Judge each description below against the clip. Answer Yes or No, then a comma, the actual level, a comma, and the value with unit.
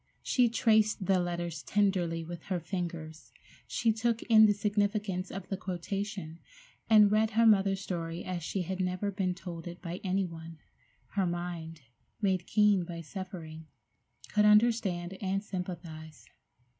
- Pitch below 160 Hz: No, medium, 185 Hz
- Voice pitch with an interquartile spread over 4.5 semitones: No, average, 3.1 semitones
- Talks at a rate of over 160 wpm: No, average, 145 wpm